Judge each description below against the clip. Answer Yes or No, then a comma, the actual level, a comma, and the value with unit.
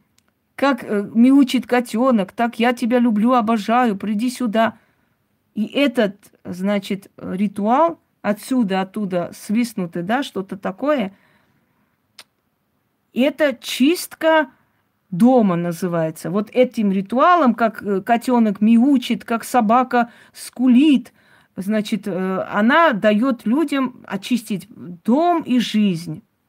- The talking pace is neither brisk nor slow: No, slow, 95 wpm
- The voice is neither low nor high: No, high, 235 Hz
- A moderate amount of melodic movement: Yes, average, 3.7 semitones